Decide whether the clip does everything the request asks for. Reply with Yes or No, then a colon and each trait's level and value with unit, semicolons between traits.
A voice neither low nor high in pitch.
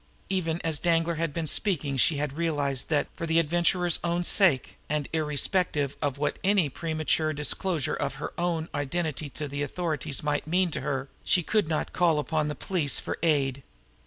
Yes: medium, 155 Hz